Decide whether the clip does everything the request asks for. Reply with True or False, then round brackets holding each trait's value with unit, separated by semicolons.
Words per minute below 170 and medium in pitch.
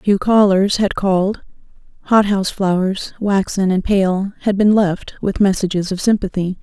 False (155 wpm; 195 Hz)